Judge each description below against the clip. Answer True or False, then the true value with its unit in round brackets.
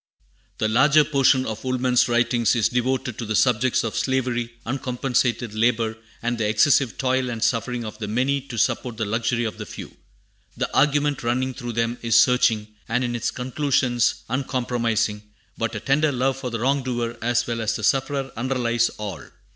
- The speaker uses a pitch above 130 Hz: False (120 Hz)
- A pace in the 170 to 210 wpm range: True (180 wpm)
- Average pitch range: False (2.2 semitones)